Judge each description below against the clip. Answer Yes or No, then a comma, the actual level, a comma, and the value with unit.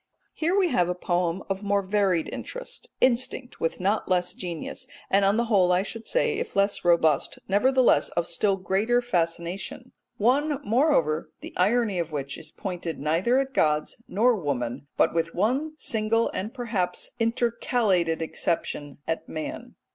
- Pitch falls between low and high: No, high, 195 Hz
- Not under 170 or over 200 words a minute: No, average, 155 wpm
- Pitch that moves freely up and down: Yes, wide, 5.9 semitones